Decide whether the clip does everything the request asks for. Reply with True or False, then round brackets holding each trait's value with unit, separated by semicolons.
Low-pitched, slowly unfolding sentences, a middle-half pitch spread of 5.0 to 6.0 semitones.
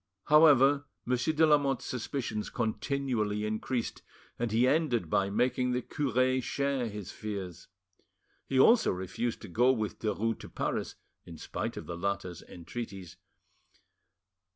False (120 Hz; 130 wpm; 4.6 semitones)